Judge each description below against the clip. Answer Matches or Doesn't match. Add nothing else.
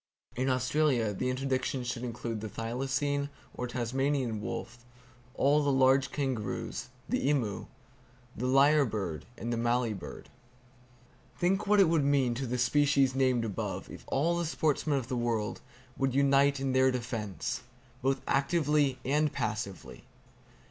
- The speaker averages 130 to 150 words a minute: Matches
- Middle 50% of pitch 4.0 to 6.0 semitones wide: Doesn't match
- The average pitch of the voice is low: Matches